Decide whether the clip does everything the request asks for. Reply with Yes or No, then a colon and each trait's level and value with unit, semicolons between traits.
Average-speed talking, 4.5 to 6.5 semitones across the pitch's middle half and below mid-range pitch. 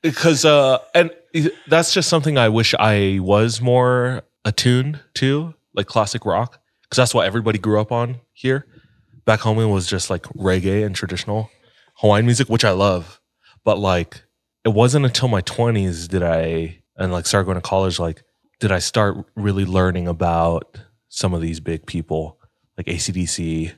Yes: average, 170 wpm; average, 5.2 semitones; low, 110 Hz